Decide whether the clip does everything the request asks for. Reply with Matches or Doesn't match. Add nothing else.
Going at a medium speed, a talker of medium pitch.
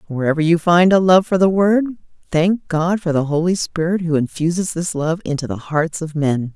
Doesn't match